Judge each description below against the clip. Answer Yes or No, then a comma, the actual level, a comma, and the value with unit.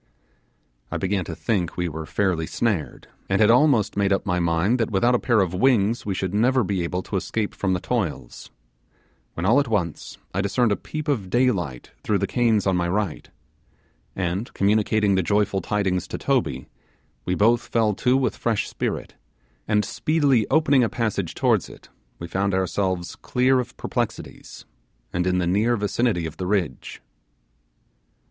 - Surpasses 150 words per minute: Yes, average, 175 wpm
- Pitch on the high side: No, low, 100 Hz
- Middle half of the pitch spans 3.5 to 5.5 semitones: Yes, average, 4.3 semitones